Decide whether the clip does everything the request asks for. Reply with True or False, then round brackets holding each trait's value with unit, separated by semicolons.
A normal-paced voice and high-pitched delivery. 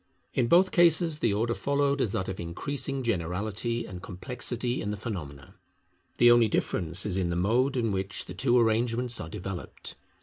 False (175 wpm; 115 Hz)